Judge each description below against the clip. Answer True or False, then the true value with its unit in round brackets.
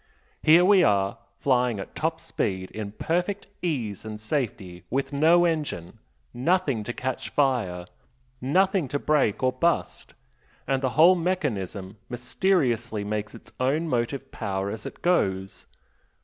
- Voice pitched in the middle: False (130 Hz)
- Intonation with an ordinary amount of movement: False (7.4 semitones)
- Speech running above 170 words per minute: False (135 wpm)